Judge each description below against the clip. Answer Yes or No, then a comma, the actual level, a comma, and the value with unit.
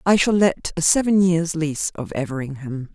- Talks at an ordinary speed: Yes, average, 185 wpm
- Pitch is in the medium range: Yes, medium, 165 Hz